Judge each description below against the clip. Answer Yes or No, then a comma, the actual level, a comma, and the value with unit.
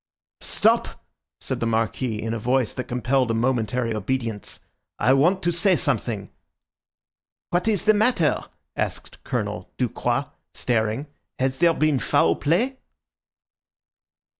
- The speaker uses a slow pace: Yes, slow, 125 wpm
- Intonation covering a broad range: Yes, wide, 6.5 semitones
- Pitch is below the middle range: Yes, low, 130 Hz